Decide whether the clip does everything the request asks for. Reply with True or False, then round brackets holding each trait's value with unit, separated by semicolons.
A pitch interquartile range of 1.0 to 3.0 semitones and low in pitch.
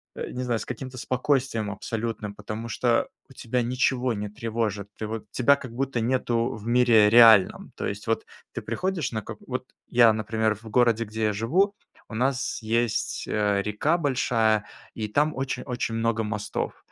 True (2.7 semitones; 115 Hz)